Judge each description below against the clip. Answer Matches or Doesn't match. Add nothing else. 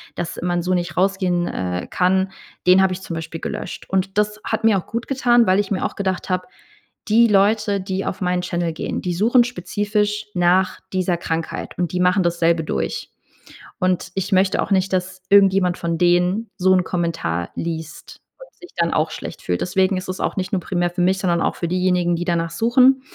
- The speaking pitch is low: Doesn't match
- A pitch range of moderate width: Doesn't match